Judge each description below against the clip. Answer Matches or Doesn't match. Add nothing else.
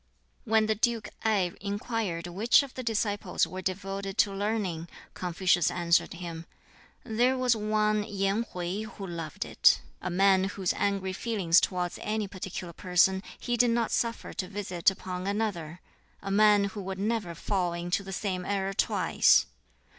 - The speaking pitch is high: Matches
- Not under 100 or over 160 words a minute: Matches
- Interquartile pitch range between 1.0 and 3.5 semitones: Matches